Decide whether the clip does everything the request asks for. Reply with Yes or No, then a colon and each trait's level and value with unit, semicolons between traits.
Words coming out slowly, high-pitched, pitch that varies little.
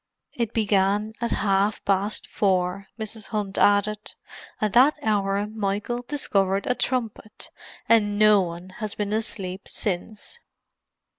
Yes: slow, 125 wpm; high, 205 Hz; narrow, 1.9 semitones